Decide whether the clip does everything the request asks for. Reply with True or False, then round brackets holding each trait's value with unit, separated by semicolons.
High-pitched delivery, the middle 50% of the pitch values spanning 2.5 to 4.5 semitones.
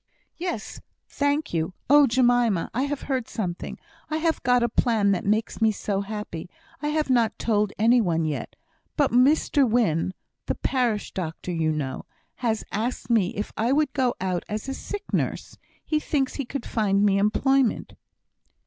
False (230 Hz; 5.1 semitones)